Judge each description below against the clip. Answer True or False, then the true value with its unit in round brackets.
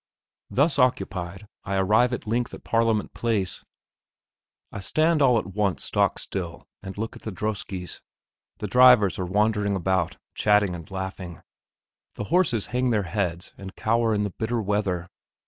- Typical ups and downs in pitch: True (3.4 semitones)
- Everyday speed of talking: True (155 wpm)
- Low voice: True (105 Hz)